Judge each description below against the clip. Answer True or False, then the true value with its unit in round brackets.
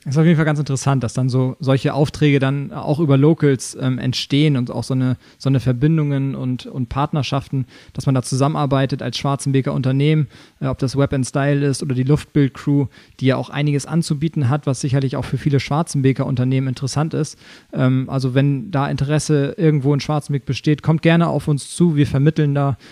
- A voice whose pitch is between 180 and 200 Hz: False (140 Hz)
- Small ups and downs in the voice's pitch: True (2.1 semitones)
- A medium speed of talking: False (205 wpm)